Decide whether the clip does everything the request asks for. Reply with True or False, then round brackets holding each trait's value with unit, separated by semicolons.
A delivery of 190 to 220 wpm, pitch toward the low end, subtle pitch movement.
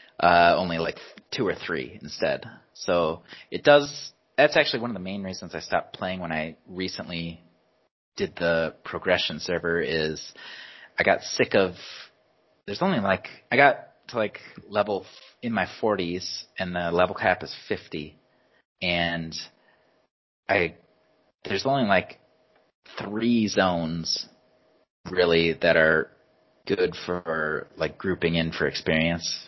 False (135 wpm; 85 Hz; 2.0 semitones)